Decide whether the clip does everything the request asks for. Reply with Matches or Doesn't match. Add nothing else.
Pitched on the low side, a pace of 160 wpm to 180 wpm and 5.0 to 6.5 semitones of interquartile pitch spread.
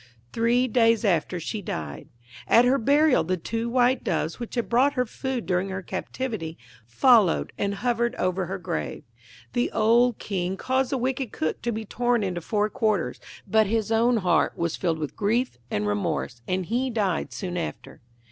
Doesn't match